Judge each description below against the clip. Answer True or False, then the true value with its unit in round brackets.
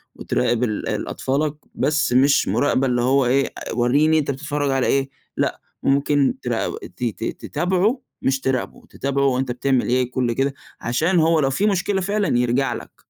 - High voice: False (135 Hz)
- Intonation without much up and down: False (3.4 semitones)